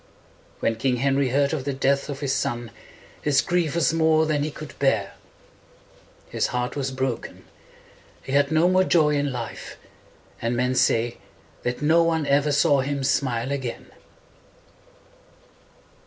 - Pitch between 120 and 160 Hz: Yes, medium, 140 Hz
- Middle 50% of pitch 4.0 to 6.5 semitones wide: No, average, 2.8 semitones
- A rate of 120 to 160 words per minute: Yes, average, 150 wpm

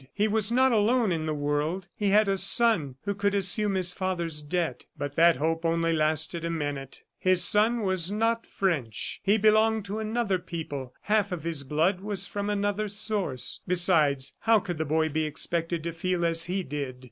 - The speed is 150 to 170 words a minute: No, average, 190 wpm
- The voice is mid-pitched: Yes, medium, 180 Hz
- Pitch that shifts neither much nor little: Yes, average, 4.5 semitones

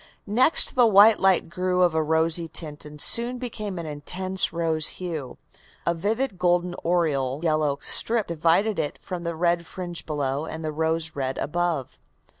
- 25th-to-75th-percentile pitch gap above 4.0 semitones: No, average, 3.0 semitones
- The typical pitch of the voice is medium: Yes, medium, 170 Hz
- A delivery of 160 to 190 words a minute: Yes, average, 165 wpm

